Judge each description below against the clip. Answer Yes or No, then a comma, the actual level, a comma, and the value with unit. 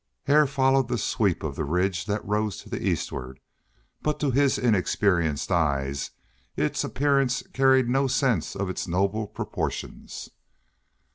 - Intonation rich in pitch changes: Yes, wide, 7.2 semitones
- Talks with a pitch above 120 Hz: No, low, 105 Hz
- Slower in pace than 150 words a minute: Yes, average, 140 wpm